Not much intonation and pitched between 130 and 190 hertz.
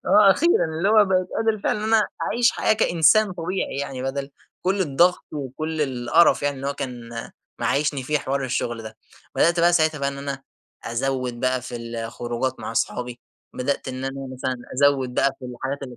No: average, 5.1 semitones; medium, 140 Hz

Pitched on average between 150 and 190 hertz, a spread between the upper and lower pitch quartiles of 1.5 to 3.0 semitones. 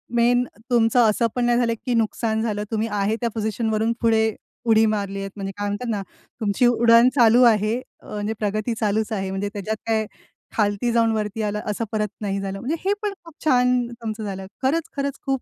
No: high, 220 Hz; narrow, 2.4 semitones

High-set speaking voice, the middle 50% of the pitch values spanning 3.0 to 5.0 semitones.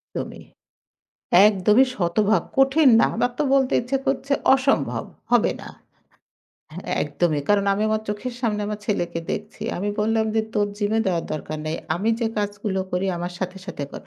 Yes: high, 210 Hz; average, 3.7 semitones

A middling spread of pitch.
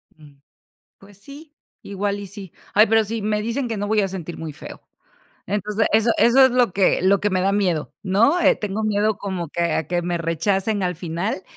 Yes: average, 3.2 semitones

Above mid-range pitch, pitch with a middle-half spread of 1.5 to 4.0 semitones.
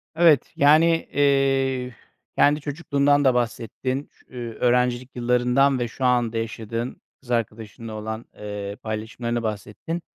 No: low, 125 Hz; average, 3.2 semitones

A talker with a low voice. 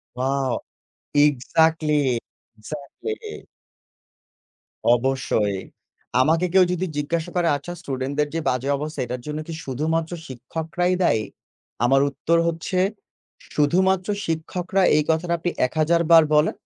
No: medium, 155 Hz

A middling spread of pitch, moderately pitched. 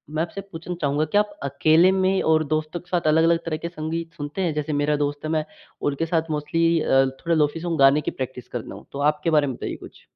No: narrow, 2.3 semitones; medium, 155 Hz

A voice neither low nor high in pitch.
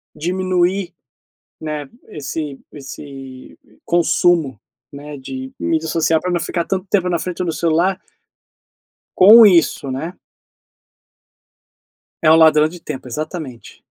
Yes: medium, 165 Hz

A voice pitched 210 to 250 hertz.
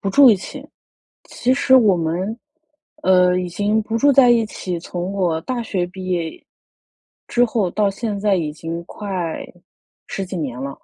No: high, 195 Hz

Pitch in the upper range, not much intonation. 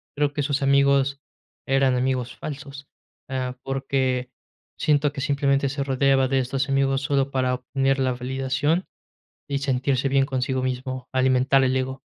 No: low, 135 Hz; narrow, 1.1 semitones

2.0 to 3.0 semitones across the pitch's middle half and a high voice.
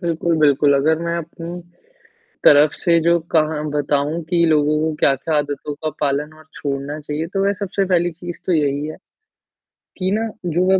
No: narrow, 2.6 semitones; medium, 155 Hz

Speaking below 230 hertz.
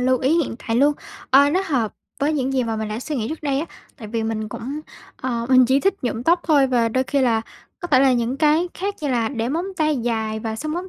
No: very high, 260 Hz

